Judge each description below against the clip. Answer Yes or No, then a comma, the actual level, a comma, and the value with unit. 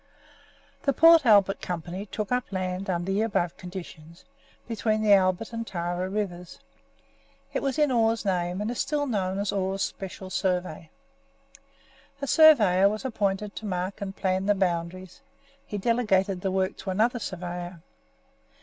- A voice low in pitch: No, high, 195 Hz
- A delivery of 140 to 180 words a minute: Yes, average, 150 wpm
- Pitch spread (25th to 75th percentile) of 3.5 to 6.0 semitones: No, average, 3.1 semitones